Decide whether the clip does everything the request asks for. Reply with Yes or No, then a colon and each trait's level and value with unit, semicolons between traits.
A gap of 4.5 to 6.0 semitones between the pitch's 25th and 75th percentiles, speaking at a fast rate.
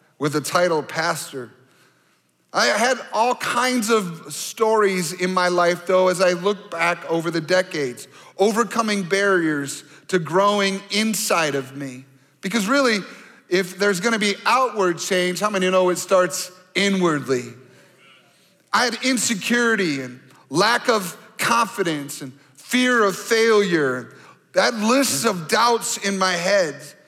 No: average, 4.8 semitones; slow, 135 wpm